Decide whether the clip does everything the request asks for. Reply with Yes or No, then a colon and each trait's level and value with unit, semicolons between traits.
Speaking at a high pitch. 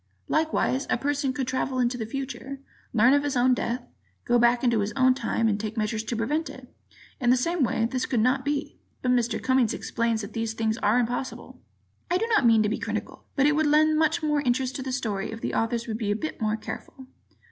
Yes: very high, 250 Hz